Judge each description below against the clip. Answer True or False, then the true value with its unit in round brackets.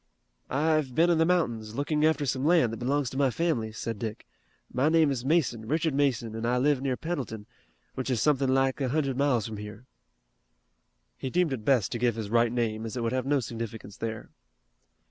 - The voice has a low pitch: True (130 Hz)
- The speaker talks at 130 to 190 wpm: False (205 wpm)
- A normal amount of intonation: True (4.2 semitones)